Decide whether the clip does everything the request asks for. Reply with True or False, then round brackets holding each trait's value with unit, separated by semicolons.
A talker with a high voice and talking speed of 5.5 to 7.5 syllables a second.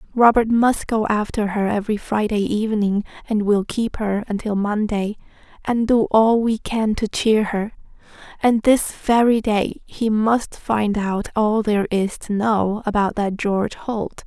False (215 Hz; 4.3 syllables/s)